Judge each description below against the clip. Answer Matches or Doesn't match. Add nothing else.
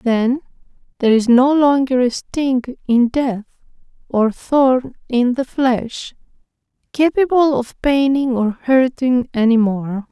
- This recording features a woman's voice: Matches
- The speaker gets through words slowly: Matches